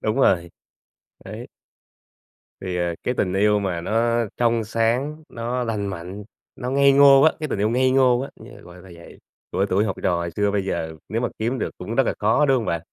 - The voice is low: Yes, low, 110 Hz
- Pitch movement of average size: Yes, average, 4.7 semitones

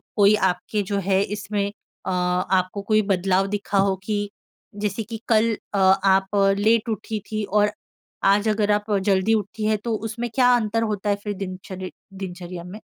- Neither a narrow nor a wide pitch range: No, narrow, 2.1 semitones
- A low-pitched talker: No, high, 205 Hz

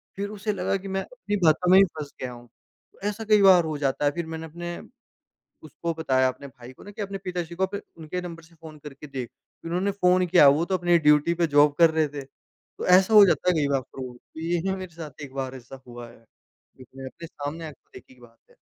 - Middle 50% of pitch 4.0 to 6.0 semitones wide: Yes, average, 4.7 semitones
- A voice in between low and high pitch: Yes, medium, 160 Hz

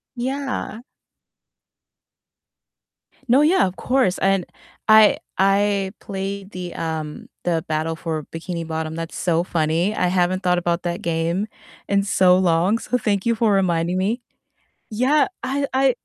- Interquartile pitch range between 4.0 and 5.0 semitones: Yes, average, 4.3 semitones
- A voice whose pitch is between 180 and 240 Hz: Yes, medium, 185 Hz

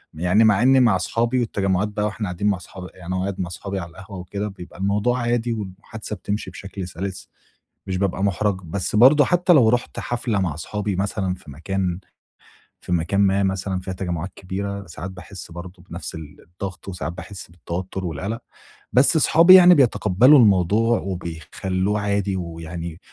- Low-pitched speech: Yes, very low, 95 Hz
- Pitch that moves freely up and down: No, average, 2.8 semitones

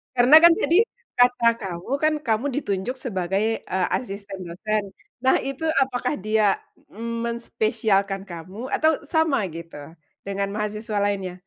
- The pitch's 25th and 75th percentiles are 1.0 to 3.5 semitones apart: No, average, 4.2 semitones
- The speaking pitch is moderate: No, high, 215 Hz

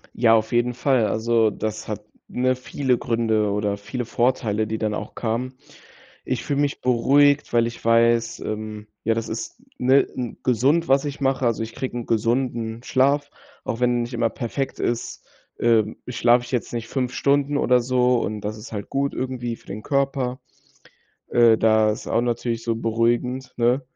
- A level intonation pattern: Yes, narrow, 2.3 semitones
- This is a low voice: Yes, low, 120 Hz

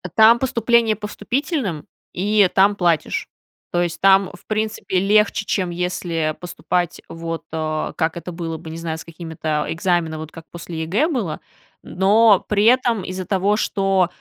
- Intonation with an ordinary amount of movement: Yes, average, 4.1 semitones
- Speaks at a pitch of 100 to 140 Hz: No, medium, 185 Hz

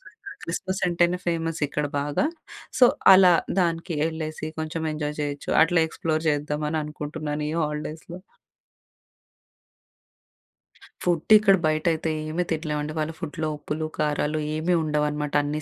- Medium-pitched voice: Yes, medium, 155 Hz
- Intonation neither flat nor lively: No, narrow, 1.9 semitones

